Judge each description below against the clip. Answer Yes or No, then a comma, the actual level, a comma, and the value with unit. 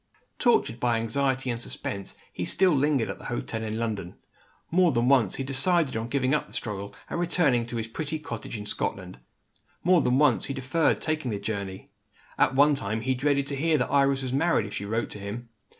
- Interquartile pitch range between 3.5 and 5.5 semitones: Yes, average, 4.4 semitones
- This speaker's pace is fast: Yes, fast, 210 wpm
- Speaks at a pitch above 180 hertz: No, low, 130 Hz